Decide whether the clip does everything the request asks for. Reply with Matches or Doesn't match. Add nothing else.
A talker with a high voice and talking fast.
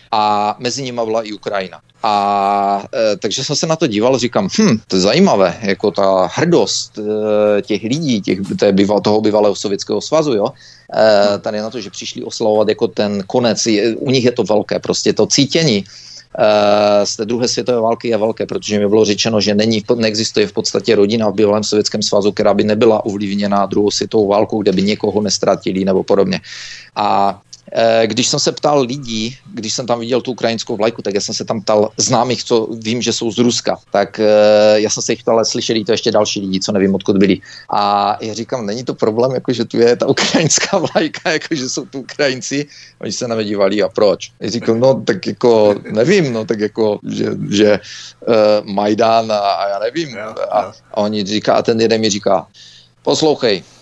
Doesn't match